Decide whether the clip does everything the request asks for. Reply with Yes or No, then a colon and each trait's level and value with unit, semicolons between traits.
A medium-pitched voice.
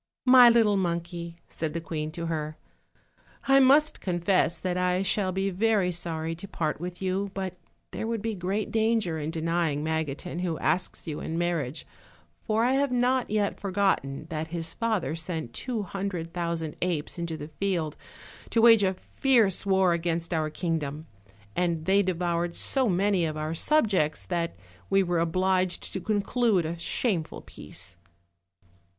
Yes: medium, 180 Hz